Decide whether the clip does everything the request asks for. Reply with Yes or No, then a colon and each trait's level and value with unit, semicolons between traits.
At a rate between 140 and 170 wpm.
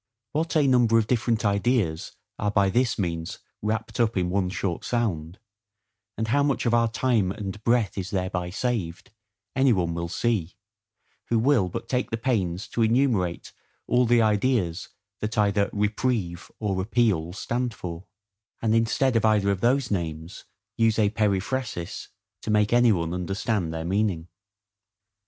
Yes: average, 155 wpm